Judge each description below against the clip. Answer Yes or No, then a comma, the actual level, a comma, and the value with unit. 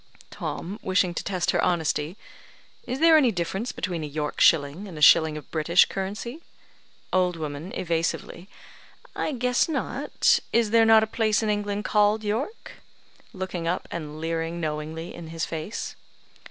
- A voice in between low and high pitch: Yes, medium, 180 Hz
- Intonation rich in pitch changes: No, average, 4.7 semitones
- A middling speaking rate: Yes, average, 155 wpm